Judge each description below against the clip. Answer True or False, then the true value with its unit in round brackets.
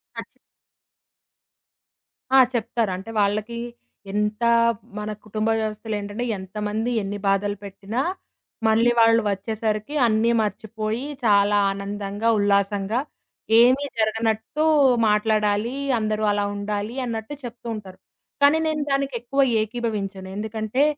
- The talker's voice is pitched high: True (215 Hz)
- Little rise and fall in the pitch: True (2.1 semitones)